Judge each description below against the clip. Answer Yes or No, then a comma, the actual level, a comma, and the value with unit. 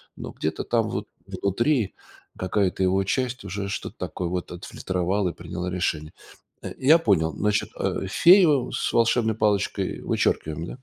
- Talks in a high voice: No, low, 100 Hz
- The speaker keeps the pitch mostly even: No, average, 4.1 semitones